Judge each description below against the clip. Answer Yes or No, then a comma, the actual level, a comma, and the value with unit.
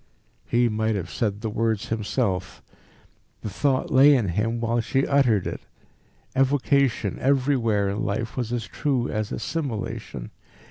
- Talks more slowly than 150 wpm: Yes, average, 140 wpm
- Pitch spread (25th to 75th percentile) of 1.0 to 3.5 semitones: No, average, 3.9 semitones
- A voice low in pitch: Yes, low, 115 Hz